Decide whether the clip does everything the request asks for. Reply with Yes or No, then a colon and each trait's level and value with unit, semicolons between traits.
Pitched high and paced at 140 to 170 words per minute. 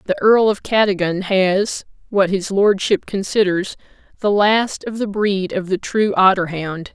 Yes: high, 195 Hz; average, 165 wpm